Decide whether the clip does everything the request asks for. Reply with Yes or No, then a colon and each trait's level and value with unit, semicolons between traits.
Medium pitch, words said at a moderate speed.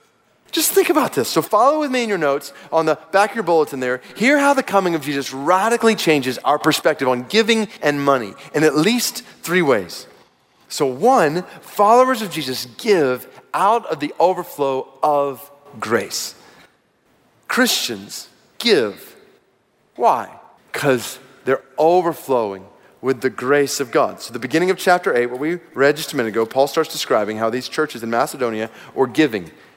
Yes: medium, 145 Hz; average, 165 wpm